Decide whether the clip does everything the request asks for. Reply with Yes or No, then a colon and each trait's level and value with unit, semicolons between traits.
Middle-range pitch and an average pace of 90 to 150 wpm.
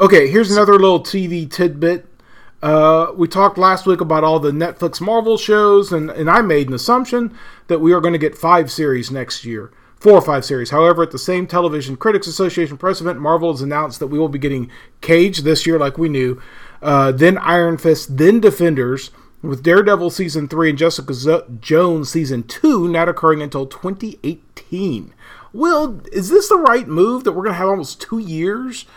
No: medium, 170 Hz; average, 195 wpm